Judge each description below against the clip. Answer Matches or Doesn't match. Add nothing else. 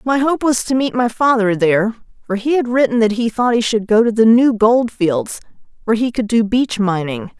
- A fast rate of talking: Matches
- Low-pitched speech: Doesn't match